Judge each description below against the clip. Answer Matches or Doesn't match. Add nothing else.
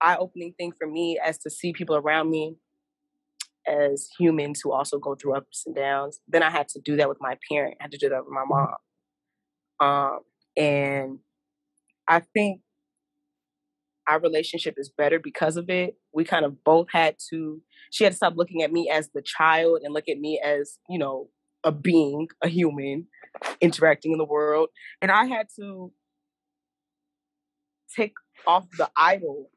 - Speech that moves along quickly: Doesn't match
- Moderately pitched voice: Matches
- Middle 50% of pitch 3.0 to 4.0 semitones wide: Doesn't match